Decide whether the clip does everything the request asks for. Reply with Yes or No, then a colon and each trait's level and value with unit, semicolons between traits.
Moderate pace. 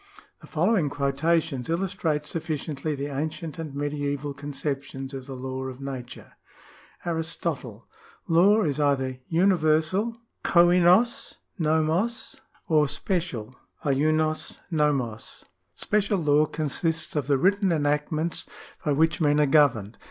No: slow, 120 wpm